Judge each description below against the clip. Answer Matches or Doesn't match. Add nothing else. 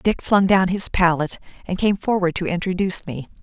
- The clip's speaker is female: Matches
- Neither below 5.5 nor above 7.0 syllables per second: Matches